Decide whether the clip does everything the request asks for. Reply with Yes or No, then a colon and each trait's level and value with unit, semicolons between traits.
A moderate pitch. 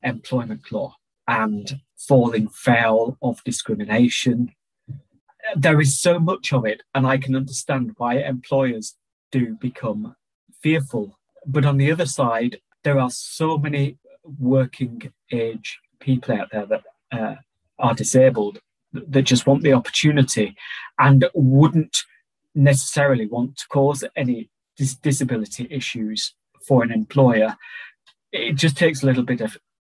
No: low, 130 Hz